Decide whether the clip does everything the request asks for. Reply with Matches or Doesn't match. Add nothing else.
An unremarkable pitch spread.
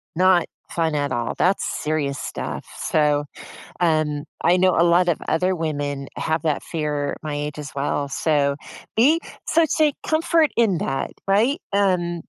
Matches